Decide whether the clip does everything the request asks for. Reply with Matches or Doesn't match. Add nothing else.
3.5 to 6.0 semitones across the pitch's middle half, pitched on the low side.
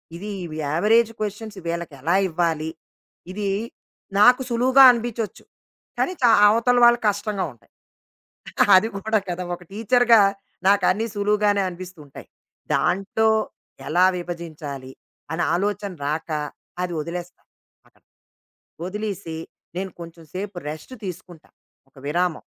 Doesn't match